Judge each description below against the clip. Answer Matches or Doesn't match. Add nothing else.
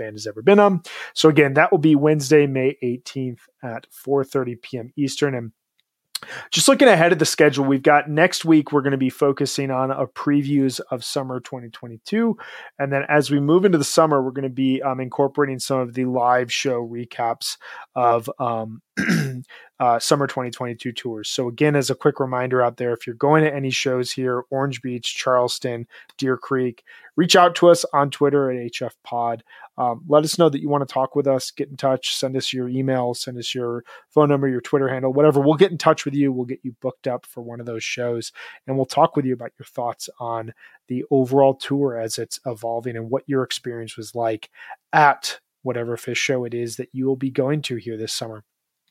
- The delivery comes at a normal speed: Doesn't match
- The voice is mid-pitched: Doesn't match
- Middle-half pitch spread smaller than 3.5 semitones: Matches